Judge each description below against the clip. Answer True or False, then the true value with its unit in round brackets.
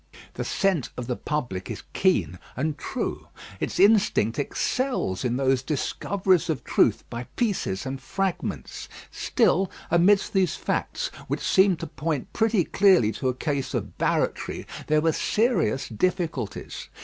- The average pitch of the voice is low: False (160 Hz)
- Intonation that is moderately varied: False (7.0 semitones)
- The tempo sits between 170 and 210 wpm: False (140 wpm)